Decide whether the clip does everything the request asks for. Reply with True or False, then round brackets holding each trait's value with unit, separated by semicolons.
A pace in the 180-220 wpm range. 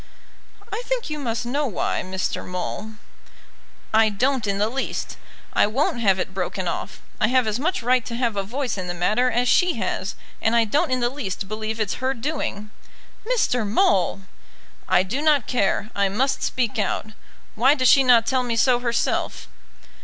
True (185 wpm)